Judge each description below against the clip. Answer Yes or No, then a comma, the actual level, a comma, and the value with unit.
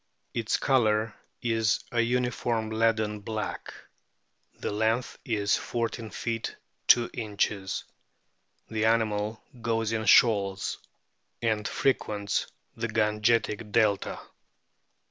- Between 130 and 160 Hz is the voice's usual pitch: No, low, 110 Hz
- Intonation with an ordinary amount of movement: No, narrow, 1.5 semitones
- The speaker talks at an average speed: No, slow, 95 wpm